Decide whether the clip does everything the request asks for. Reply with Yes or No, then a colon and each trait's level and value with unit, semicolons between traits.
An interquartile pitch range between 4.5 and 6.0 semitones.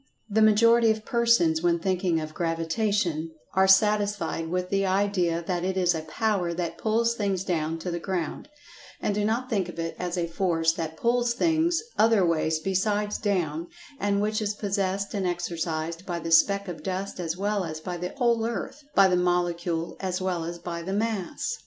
No: average, 3.7 semitones